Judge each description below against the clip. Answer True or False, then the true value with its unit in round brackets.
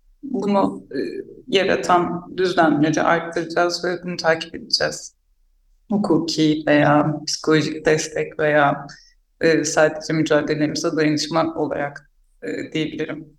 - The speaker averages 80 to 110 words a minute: True (100 wpm)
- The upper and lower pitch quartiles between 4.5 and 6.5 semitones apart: False (2.4 semitones)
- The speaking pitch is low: False (155 Hz)